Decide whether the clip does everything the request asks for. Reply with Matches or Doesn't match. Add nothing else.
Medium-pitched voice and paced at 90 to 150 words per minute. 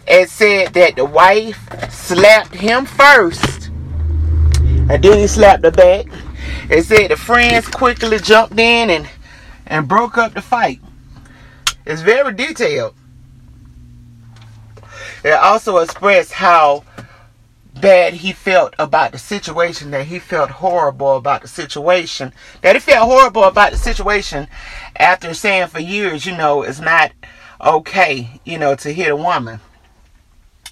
Matches